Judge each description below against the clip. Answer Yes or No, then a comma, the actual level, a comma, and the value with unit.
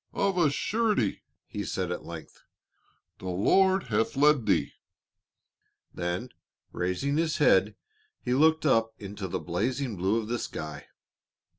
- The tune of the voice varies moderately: No, wide, 8.1 semitones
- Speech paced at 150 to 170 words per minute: No, slow, 135 wpm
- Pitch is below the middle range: Yes, low, 115 Hz